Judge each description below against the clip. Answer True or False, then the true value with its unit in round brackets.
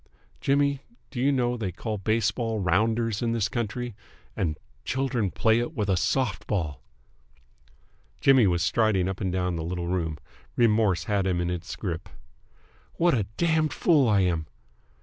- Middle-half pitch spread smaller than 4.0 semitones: False (5.0 semitones)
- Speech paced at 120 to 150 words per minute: False (160 wpm)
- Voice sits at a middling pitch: False (105 Hz)